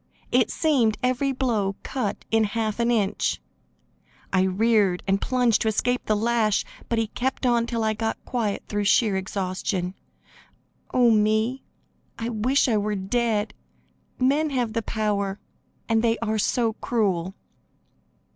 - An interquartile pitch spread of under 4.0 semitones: Yes, narrow, 2.6 semitones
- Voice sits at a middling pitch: No, high, 220 Hz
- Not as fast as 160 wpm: Yes, average, 145 wpm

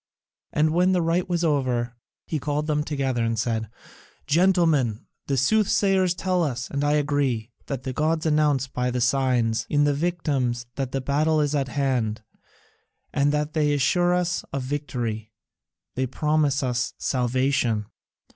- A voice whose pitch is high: No, medium, 140 Hz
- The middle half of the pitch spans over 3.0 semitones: Yes, average, 3.7 semitones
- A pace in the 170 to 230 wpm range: No, average, 150 wpm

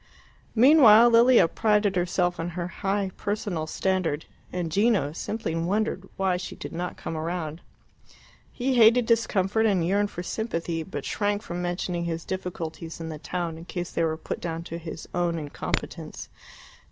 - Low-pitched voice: No, medium, 180 Hz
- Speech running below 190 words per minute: Yes, average, 160 wpm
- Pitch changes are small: No, average, 3.8 semitones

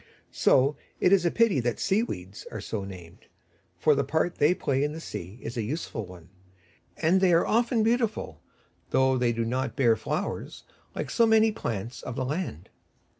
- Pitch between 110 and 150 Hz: Yes, low, 135 Hz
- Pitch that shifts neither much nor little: No, wide, 8.8 semitones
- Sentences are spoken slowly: No, average, 185 wpm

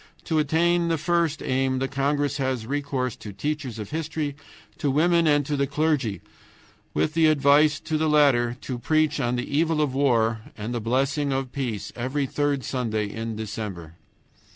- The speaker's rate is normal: Yes, average, 175 wpm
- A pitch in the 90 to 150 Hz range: Yes, medium, 140 Hz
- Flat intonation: No, average, 3.9 semitones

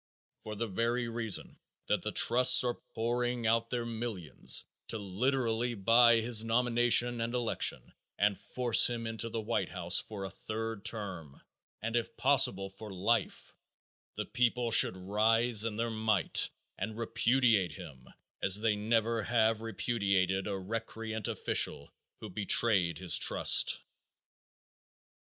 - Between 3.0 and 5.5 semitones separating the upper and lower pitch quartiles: No, narrow, 2.4 semitones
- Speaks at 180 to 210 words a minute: No, slow, 135 wpm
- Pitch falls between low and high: No, low, 115 Hz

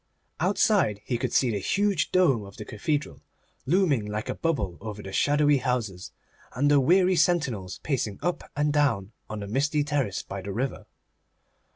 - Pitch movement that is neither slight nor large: No, wide, 6.7 semitones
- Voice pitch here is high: No, low, 135 Hz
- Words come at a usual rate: Yes, average, 170 wpm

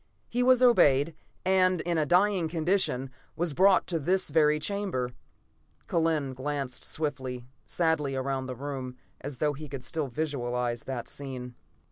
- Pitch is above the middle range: No, medium, 145 Hz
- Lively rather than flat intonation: No, average, 4.7 semitones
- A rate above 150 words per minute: No, average, 145 wpm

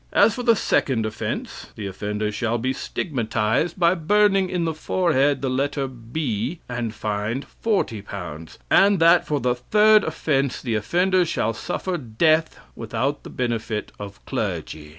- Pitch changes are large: Yes, wide, 7.4 semitones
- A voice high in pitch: No, low, 135 Hz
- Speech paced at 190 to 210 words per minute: No, average, 150 wpm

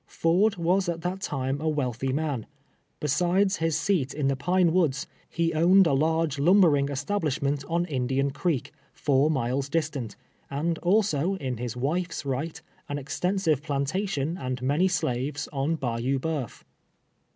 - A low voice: No, medium, 150 Hz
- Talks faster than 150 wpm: No, average, 145 wpm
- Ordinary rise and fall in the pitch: Yes, average, 4.1 semitones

